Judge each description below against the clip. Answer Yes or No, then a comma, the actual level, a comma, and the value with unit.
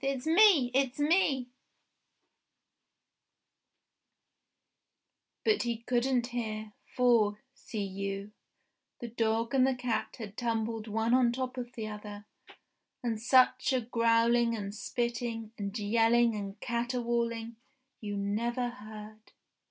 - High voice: Yes, high, 235 Hz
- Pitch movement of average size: No, narrow, 2.3 semitones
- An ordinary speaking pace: No, slow, 120 wpm